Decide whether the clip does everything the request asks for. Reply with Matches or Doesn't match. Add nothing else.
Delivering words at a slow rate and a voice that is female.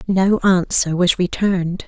Matches